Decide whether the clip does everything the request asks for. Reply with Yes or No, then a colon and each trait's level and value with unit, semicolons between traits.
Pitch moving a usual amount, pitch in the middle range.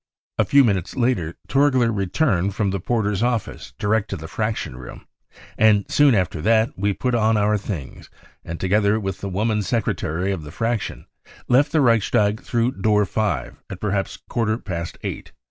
No: average, 3.3 semitones; low, 105 Hz